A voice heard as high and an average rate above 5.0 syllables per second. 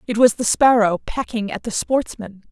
No: high, 225 Hz; 4.9 syllables/s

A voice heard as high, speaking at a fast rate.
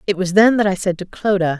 Yes: high, 195 Hz; fast, 300 wpm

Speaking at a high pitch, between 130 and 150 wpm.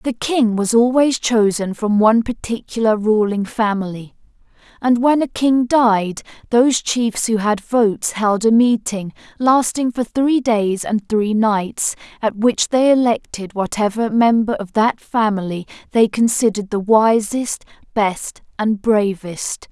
Yes: high, 225 Hz; average, 140 wpm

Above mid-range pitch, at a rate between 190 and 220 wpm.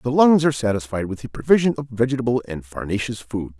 No: low, 120 Hz; average, 200 wpm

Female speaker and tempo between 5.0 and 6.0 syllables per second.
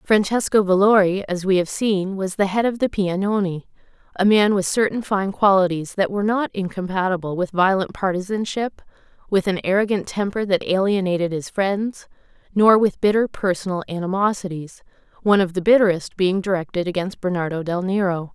Yes: female; 5.4 syllables/s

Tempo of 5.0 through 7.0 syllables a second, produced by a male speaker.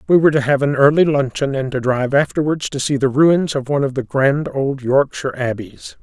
Yes: 5.6 syllables/s; male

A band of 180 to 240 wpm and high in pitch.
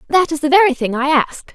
No: fast, 270 wpm; very high, 300 Hz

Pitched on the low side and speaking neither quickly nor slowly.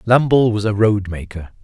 Yes: low, 105 Hz; average, 145 wpm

